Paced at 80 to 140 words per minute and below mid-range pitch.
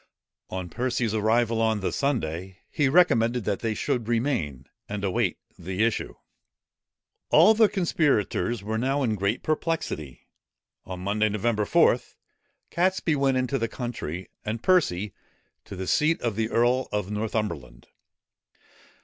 Yes: slow, 135 wpm; low, 110 Hz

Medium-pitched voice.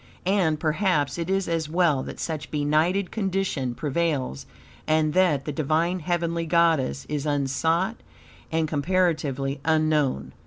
Yes: medium, 160 Hz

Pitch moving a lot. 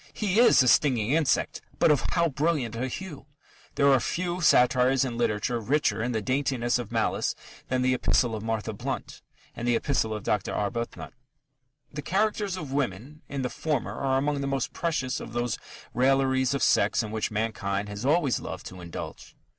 No: average, 4.2 semitones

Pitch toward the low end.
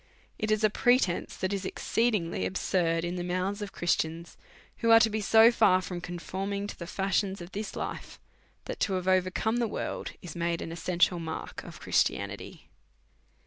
No: medium, 185 Hz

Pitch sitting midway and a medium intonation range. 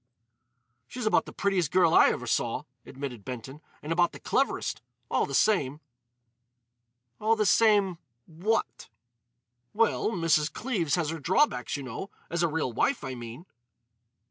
No: medium, 165 Hz; wide, 6.9 semitones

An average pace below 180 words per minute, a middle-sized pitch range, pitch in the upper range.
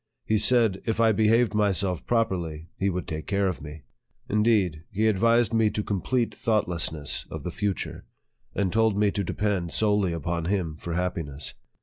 No: average, 170 wpm; average, 4.1 semitones; low, 100 Hz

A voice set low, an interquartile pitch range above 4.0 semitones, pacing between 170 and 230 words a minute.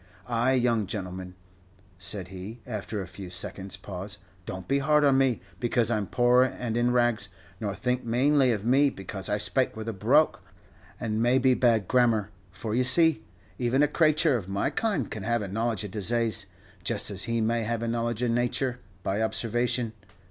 No: low, 115 Hz; average, 3.4 semitones; average, 185 wpm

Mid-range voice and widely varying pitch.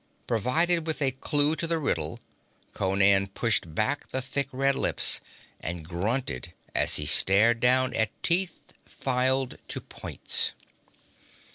No: low, 125 Hz; wide, 6.2 semitones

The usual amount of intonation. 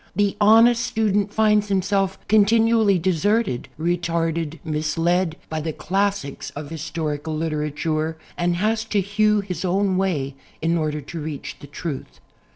Yes: average, 4.5 semitones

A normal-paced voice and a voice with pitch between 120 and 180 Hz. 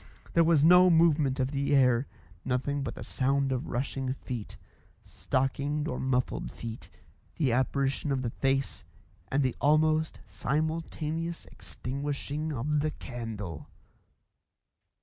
No: slow, 125 wpm; medium, 140 Hz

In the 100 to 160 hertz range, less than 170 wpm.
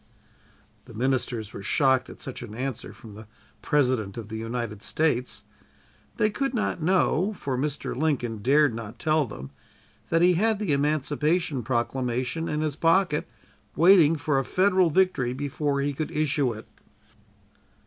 Yes: medium, 140 Hz; average, 150 wpm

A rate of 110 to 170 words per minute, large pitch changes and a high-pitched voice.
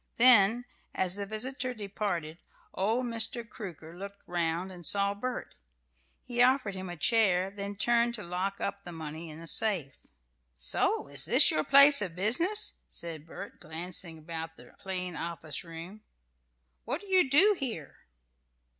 Yes: average, 155 wpm; wide, 5.8 semitones; high, 195 Hz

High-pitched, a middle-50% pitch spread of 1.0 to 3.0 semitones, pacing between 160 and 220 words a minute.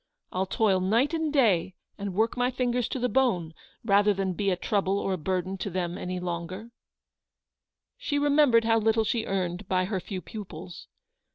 No: high, 200 Hz; average, 4.0 semitones; average, 180 wpm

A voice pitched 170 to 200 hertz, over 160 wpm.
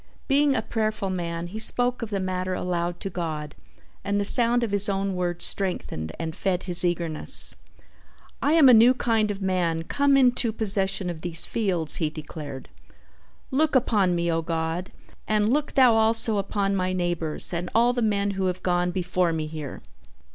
Yes: high, 190 Hz; average, 180 wpm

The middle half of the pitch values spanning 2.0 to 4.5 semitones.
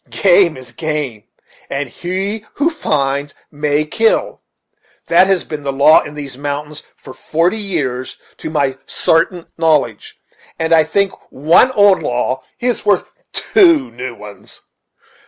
No: wide, 5.5 semitones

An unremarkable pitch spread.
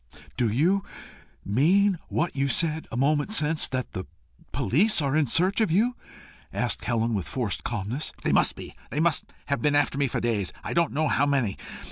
No: wide, 5.7 semitones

